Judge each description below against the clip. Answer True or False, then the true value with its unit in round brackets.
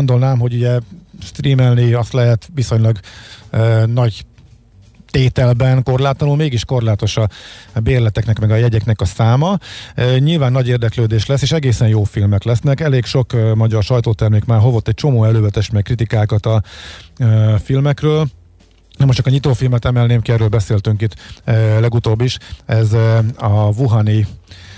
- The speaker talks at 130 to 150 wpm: True (145 wpm)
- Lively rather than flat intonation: False (2.7 semitones)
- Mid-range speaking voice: False (115 Hz)